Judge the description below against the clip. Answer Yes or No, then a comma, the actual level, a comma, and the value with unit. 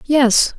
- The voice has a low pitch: No, very high, 265 Hz